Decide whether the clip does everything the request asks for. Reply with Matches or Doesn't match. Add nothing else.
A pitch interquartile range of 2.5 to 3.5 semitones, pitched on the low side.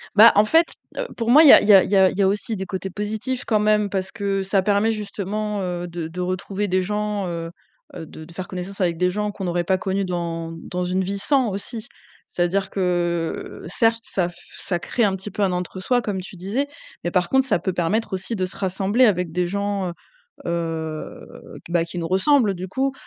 Doesn't match